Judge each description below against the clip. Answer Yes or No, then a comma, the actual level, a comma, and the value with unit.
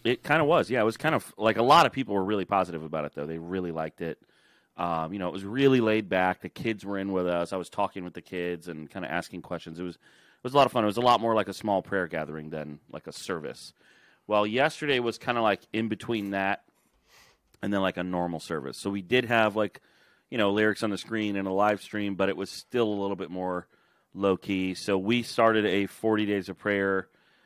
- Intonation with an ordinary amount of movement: Yes, average, 3.2 semitones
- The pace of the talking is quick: Yes, fast, 260 wpm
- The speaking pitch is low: Yes, very low, 95 Hz